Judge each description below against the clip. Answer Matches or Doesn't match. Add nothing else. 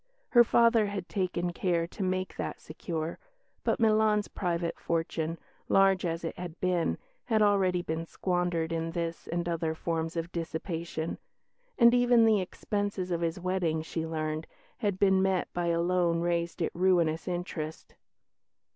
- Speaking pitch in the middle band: Matches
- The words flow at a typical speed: Matches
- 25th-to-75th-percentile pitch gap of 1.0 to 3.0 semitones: Matches